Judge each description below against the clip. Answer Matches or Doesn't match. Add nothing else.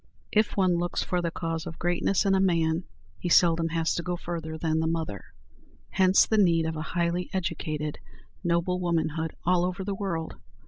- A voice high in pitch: Doesn't match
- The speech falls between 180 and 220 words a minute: Matches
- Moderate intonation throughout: Doesn't match